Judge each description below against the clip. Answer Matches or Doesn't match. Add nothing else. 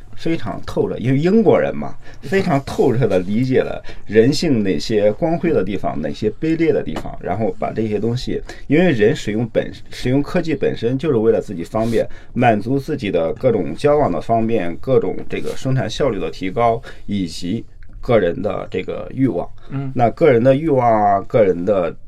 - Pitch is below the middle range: Matches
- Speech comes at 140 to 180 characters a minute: Doesn't match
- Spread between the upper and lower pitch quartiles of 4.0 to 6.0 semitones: Matches